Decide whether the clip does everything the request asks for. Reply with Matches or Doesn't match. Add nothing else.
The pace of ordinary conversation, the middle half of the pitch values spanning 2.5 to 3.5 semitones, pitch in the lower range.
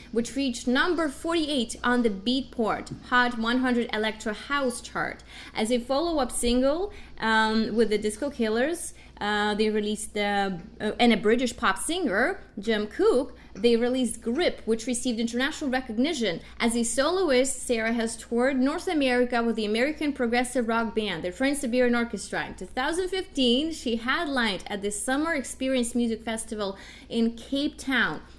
Doesn't match